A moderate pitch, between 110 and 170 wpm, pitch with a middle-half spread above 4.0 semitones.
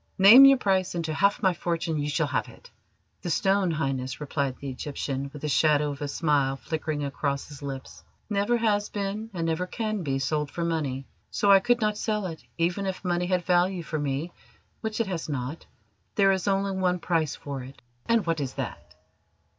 No: medium, 165 Hz; average, 200 wpm; average, 5.2 semitones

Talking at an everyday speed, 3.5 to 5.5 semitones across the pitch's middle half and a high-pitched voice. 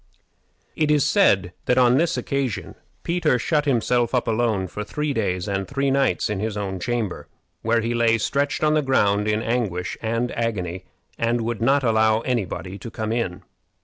No: average, 180 wpm; average, 4.3 semitones; low, 115 Hz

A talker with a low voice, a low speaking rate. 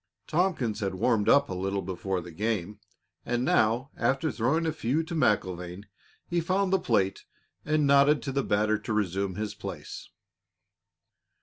No: low, 110 Hz; average, 160 wpm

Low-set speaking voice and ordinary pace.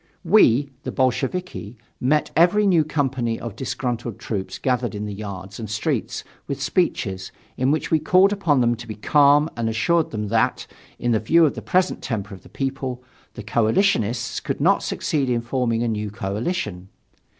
Yes: low, 125 Hz; average, 175 wpm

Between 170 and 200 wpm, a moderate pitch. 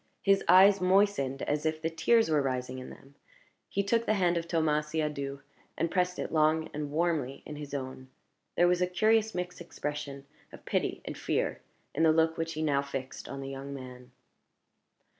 Yes: average, 190 wpm; medium, 155 Hz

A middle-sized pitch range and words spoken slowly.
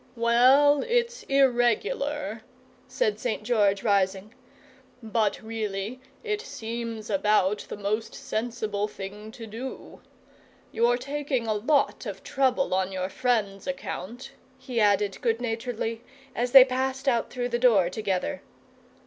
Yes: average, 3.9 semitones; slow, 125 wpm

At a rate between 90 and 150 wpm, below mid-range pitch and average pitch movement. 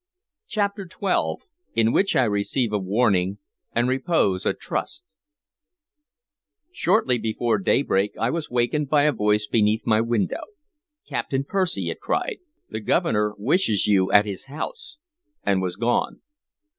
No: slow, 135 wpm; low, 115 Hz; wide, 6.1 semitones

